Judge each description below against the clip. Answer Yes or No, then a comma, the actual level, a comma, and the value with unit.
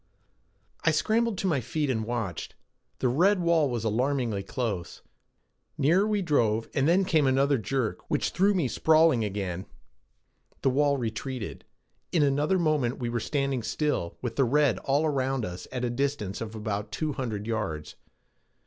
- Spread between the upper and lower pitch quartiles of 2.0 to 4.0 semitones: No, average, 5.3 semitones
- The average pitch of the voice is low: Yes, low, 130 Hz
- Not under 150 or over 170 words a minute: Yes, average, 160 wpm